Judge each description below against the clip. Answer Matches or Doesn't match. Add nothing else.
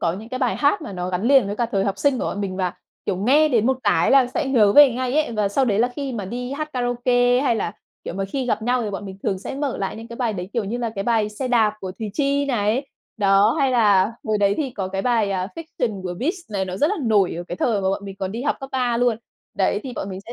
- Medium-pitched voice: Doesn't match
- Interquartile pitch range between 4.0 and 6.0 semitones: Matches